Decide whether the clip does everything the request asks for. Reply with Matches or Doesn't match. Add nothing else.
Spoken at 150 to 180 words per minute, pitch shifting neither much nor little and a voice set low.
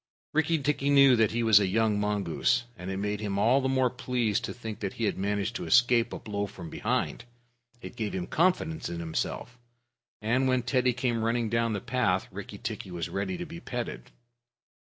Doesn't match